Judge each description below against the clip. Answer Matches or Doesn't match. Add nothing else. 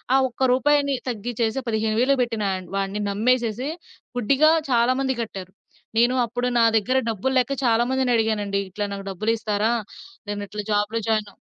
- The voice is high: Matches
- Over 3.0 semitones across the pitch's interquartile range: Matches